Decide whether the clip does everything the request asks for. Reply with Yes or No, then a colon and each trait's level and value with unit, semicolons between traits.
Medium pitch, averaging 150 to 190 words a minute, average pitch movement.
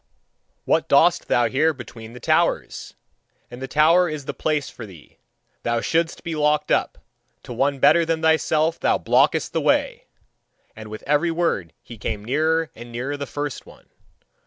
Yes: medium, 145 Hz; average, 170 wpm; average, 5.0 semitones